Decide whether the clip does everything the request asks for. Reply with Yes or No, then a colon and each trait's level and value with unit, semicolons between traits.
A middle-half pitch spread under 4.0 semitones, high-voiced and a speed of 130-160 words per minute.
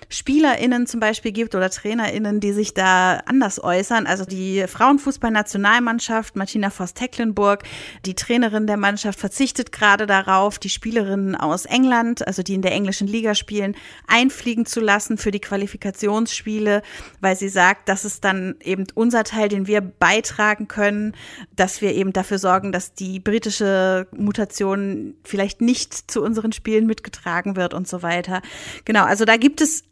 Yes: average, 2.7 semitones; high, 205 Hz; average, 155 wpm